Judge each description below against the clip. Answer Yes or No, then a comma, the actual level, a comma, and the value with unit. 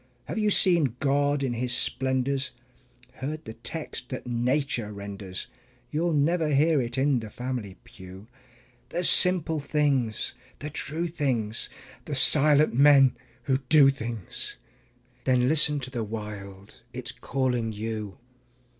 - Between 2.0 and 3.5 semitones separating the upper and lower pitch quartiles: No, average, 4.6 semitones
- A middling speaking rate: No, slow, 130 wpm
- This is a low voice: Yes, low, 130 Hz